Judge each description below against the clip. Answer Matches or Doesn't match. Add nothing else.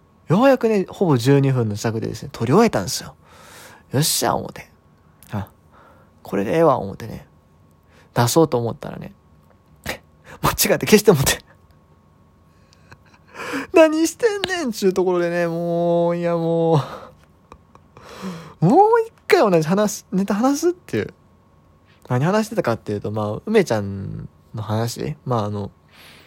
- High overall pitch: Doesn't match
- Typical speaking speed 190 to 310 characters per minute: Matches